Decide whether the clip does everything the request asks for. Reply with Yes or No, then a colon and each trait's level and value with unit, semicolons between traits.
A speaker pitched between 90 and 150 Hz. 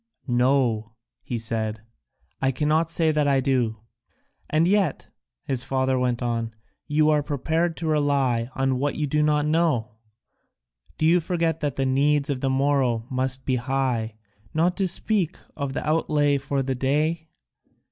Yes: medium, 140 Hz